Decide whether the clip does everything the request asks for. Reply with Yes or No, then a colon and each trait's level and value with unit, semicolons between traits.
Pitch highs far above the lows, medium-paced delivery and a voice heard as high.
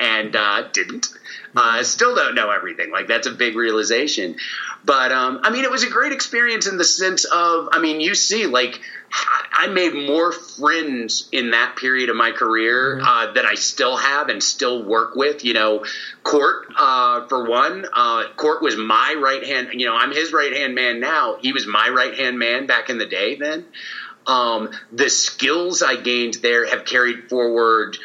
No: wide, 7.1 semitones; average, 195 wpm; low, 135 Hz